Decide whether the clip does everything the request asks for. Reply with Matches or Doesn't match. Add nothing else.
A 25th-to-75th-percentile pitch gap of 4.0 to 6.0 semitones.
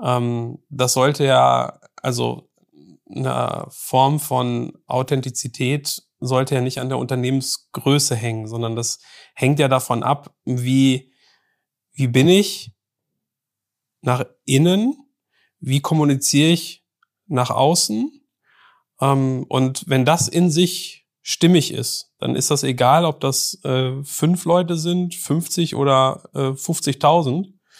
Matches